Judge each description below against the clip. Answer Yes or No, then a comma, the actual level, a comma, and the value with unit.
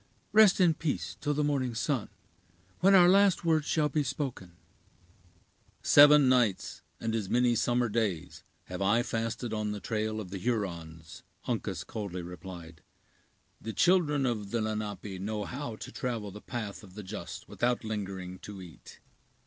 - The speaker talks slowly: No, average, 155 wpm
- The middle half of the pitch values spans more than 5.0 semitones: Yes, wide, 5.5 semitones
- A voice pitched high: No, low, 110 Hz